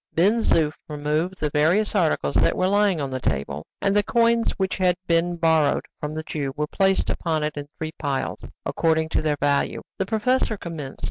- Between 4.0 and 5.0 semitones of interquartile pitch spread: Yes, average, 4.3 semitones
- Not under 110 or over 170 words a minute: No, average, 200 wpm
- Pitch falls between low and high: Yes, medium, 165 Hz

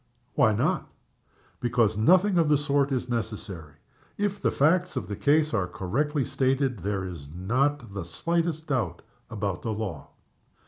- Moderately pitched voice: No, low, 125 Hz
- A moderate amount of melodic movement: No, wide, 6.9 semitones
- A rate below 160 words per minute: Yes, average, 150 wpm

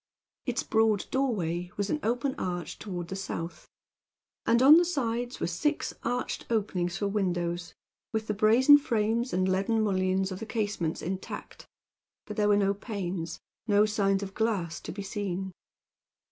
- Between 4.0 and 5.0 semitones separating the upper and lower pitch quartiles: No, average, 3.4 semitones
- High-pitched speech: Yes, high, 205 Hz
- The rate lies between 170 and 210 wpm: No, average, 160 wpm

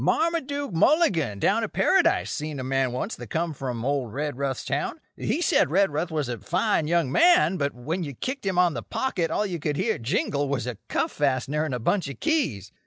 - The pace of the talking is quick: Yes, fast, 210 wpm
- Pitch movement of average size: No, wide, 5.7 semitones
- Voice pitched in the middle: Yes, medium, 150 Hz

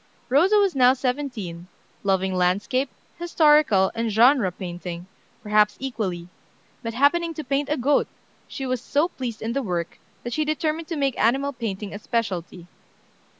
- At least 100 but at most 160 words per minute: Yes, average, 150 wpm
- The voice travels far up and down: Yes, wide, 6.4 semitones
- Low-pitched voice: No, high, 245 Hz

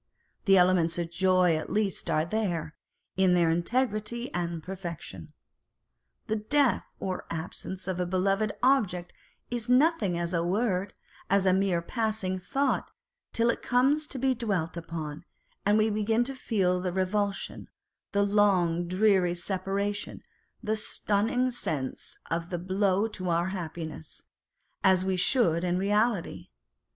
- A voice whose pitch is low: No, high, 190 Hz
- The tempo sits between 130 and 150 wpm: Yes, average, 140 wpm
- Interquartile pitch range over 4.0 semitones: No, average, 3.6 semitones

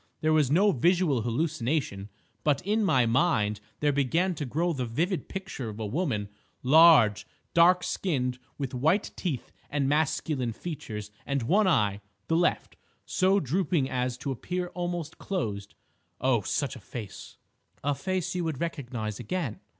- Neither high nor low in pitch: Yes, medium, 145 Hz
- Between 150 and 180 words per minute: No, average, 140 wpm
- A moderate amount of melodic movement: No, wide, 6.6 semitones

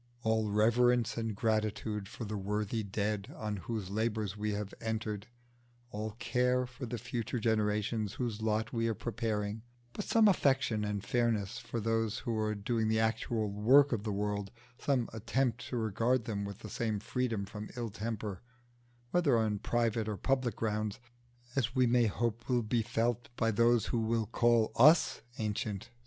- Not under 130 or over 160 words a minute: No, average, 170 wpm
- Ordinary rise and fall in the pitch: No, narrow, 2.1 semitones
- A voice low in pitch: Yes, low, 110 Hz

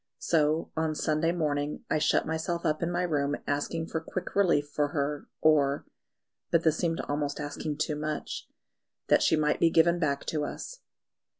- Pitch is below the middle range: No, medium, 155 Hz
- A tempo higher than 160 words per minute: Yes, average, 175 wpm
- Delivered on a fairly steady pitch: Yes, narrow, 2.0 semitones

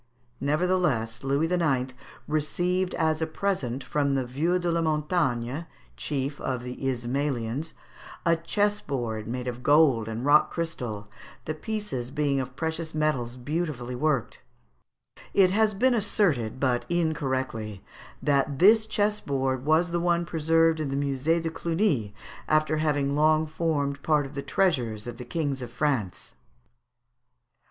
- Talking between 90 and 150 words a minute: Yes, average, 140 wpm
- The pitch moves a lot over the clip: No, average, 4.4 semitones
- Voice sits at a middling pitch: Yes, medium, 145 Hz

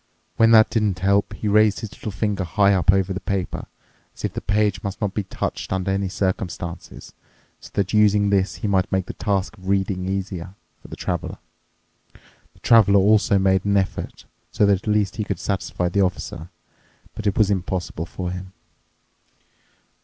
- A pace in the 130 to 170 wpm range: No, average, 185 wpm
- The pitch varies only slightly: Yes, narrow, 1.7 semitones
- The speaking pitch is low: Yes, low, 100 Hz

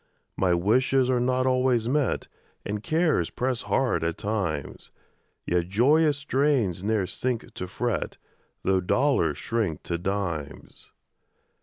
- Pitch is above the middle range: No, low, 115 Hz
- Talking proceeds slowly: Yes, slow, 125 wpm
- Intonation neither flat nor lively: No, wide, 6.1 semitones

